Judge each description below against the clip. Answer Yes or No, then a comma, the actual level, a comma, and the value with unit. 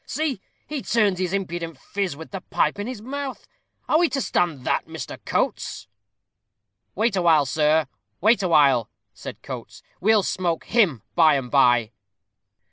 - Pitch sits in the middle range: Yes, medium, 180 Hz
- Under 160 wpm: Yes, average, 150 wpm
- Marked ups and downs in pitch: Yes, wide, 6.3 semitones